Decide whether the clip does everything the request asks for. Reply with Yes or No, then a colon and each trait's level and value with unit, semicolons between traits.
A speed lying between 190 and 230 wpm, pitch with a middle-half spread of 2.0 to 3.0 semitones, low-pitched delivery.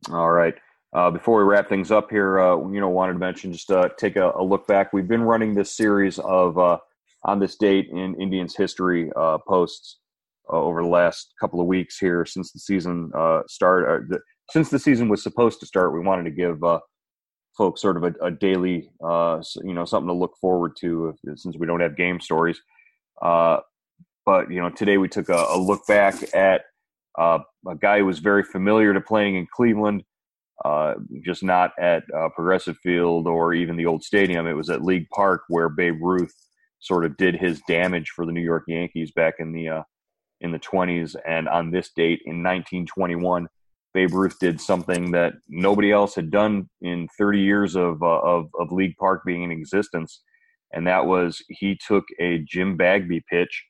Yes: average, 200 wpm; narrow, 2.4 semitones; very low, 90 Hz